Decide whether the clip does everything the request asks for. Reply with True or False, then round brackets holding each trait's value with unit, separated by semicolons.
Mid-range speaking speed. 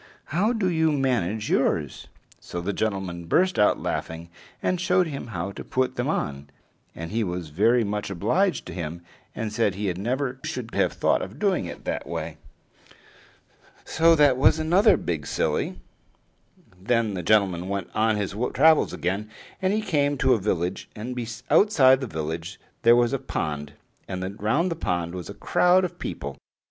True (170 wpm)